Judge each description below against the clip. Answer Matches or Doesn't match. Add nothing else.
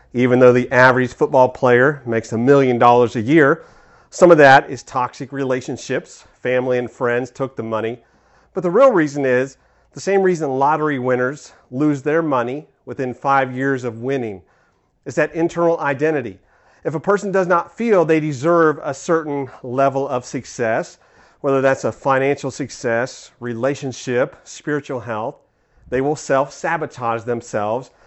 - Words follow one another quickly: Doesn't match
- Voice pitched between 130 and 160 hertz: Matches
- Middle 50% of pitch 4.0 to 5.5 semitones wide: Doesn't match